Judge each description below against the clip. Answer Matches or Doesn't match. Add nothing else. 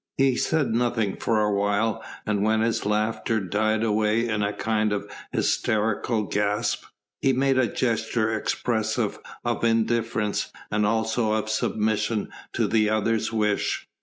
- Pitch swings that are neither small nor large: Doesn't match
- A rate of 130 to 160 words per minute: Matches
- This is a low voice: Matches